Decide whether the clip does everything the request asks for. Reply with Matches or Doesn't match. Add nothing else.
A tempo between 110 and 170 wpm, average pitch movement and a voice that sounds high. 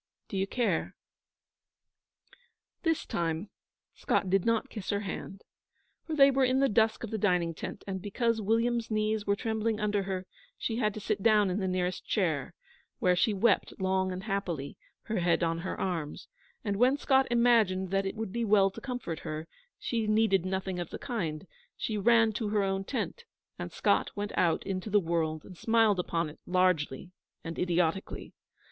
Doesn't match